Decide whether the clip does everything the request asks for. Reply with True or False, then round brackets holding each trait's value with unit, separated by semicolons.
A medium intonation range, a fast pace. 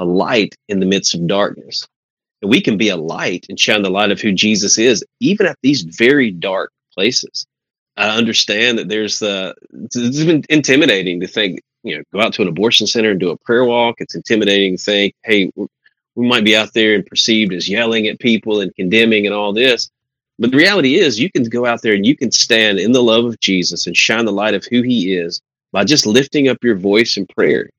True (3.0 semitones; 225 wpm)